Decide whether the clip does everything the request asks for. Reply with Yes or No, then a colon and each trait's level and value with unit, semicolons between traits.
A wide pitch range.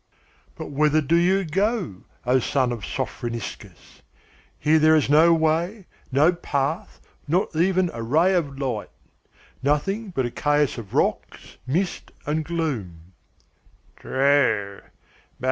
No: average, 4.5 semitones